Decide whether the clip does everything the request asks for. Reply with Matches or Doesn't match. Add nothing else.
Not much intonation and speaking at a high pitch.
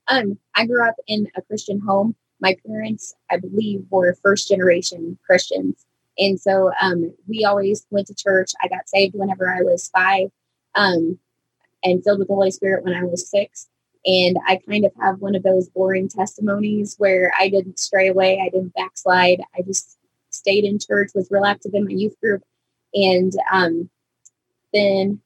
Matches